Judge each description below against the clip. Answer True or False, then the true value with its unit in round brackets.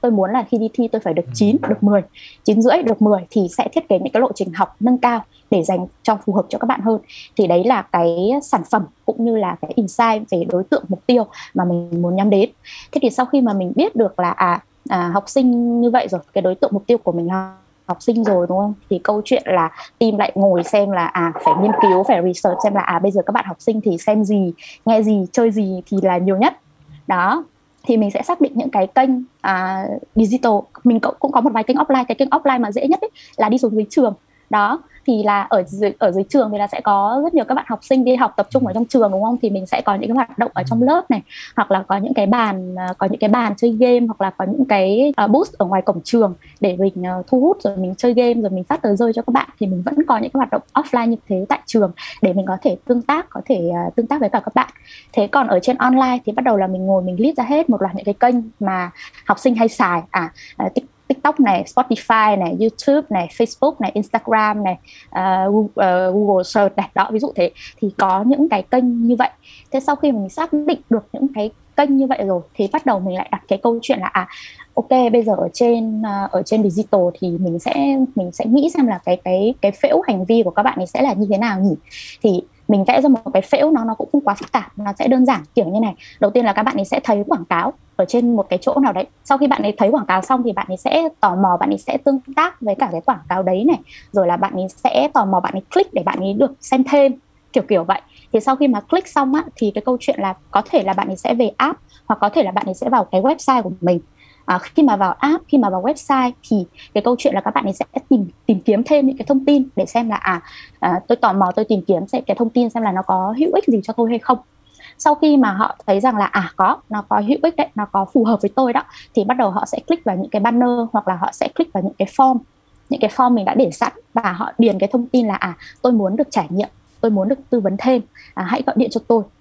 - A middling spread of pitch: True (4.9 semitones)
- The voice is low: False (220 Hz)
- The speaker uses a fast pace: True (280 wpm)